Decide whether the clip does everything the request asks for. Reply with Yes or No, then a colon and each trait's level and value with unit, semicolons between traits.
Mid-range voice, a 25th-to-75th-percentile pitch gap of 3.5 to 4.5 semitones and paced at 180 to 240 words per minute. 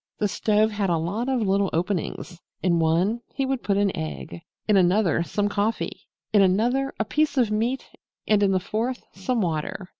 No: high, 205 Hz; average, 3.8 semitones; average, 185 wpm